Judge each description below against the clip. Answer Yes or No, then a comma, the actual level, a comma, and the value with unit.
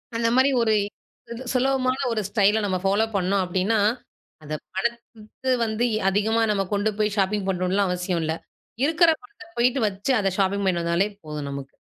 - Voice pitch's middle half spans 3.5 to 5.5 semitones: Yes, average, 3.9 semitones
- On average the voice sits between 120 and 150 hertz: No, high, 205 Hz